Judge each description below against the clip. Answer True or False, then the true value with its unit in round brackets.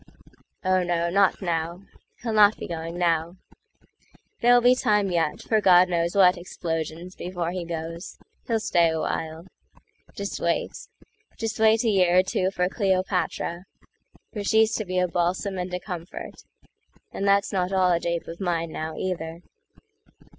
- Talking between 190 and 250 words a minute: False (140 wpm)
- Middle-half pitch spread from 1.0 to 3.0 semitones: True (2.7 semitones)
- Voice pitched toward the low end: False (180 Hz)